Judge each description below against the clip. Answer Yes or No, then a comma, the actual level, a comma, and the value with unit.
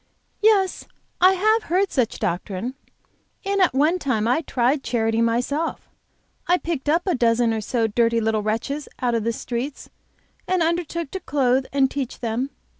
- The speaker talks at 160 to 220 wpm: Yes, average, 170 wpm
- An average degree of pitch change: No, wide, 6.6 semitones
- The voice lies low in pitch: No, very high, 265 Hz